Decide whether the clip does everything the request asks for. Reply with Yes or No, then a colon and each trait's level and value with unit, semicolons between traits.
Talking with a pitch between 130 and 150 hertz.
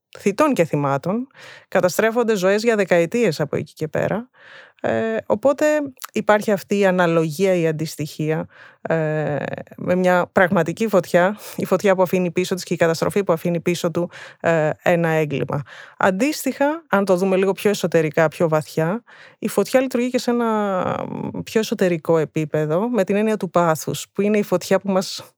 No: medium, 185 Hz